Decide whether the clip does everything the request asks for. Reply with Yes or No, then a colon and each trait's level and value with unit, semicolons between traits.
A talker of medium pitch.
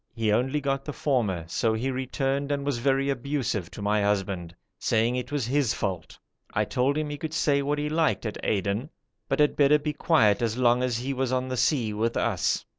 No: low, 130 Hz